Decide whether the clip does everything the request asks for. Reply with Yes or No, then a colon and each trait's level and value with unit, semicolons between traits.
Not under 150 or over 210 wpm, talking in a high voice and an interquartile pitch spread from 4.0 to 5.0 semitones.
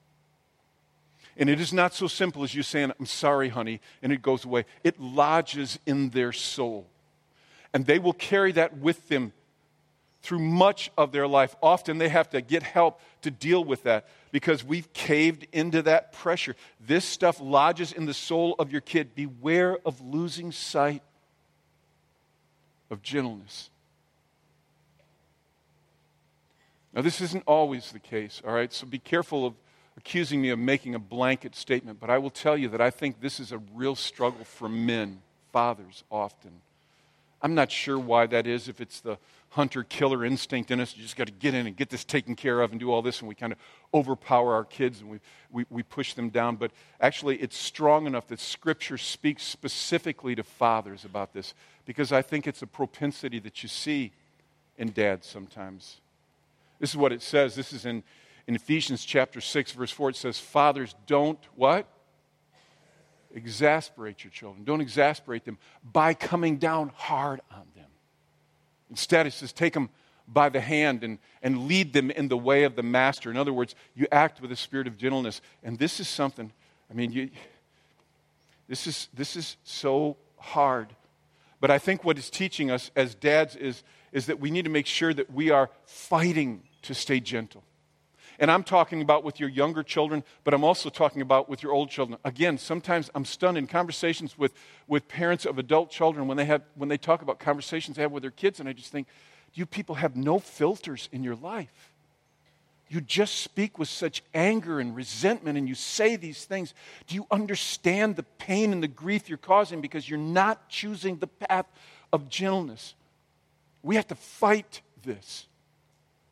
No: average, 185 wpm; medium, 140 Hz; average, 4.5 semitones